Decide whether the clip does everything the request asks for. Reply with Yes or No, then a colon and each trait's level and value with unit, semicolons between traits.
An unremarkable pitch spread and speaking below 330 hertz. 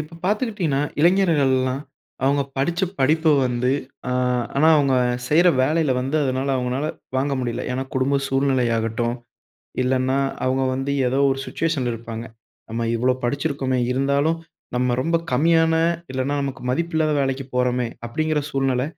Yes: average, 3.3 semitones; low, 135 Hz